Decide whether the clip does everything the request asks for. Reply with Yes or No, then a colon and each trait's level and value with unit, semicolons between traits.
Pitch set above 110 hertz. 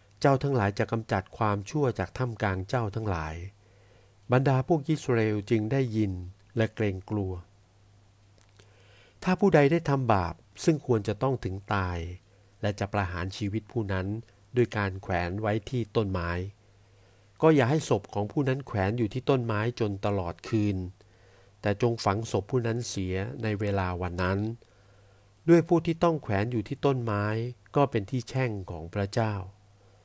No: low, 105 Hz